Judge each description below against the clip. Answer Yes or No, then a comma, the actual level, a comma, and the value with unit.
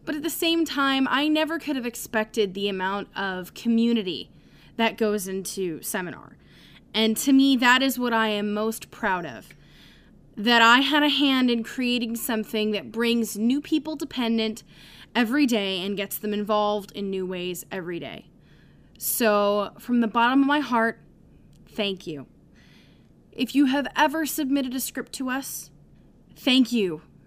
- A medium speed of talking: Yes, average, 160 wpm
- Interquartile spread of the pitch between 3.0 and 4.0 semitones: No, average, 4.4 semitones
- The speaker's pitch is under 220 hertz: No, high, 230 Hz